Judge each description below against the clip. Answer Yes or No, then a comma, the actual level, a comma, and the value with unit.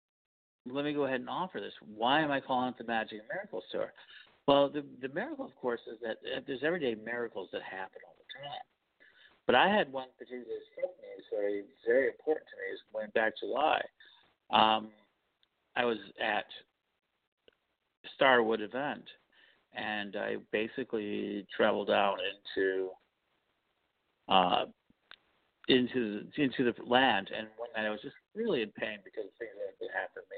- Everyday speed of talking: Yes, average, 160 wpm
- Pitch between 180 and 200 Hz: No, low, 130 Hz